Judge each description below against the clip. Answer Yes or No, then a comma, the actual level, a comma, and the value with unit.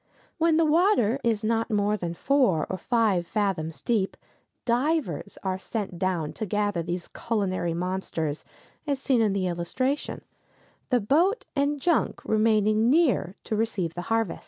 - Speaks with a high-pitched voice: Yes, high, 215 Hz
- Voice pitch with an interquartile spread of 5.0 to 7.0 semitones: Yes, wide, 5.5 semitones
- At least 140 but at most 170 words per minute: Yes, average, 150 wpm